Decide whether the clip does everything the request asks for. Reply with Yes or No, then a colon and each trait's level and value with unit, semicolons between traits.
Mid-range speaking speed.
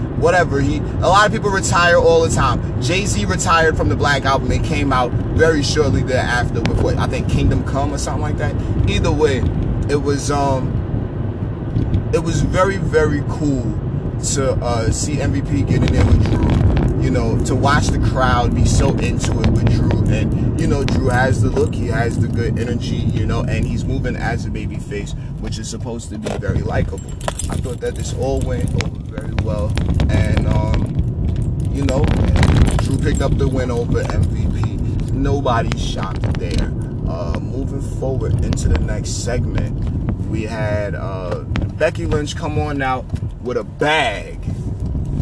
Yes: average, 175 wpm